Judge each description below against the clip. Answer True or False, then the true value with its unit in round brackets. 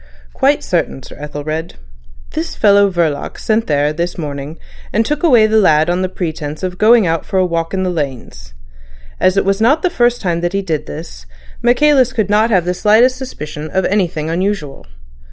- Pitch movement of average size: False (5.9 semitones)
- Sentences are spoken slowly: False (190 wpm)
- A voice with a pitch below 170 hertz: False (180 Hz)